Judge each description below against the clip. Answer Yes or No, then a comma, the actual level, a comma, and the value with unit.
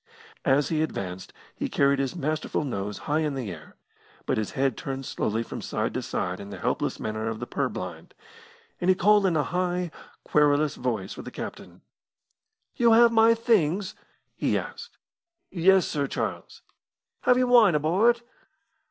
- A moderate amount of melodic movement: No, wide, 6.9 semitones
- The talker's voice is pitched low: No, medium, 150 Hz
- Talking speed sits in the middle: Yes, average, 165 wpm